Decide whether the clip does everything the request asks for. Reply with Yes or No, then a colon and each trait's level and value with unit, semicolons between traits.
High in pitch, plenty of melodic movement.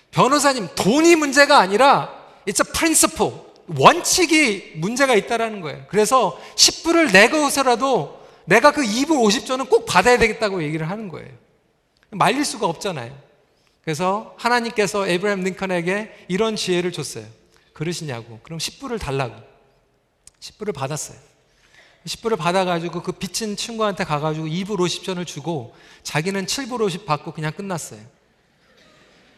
Yes: high, 195 Hz; wide, 7.0 semitones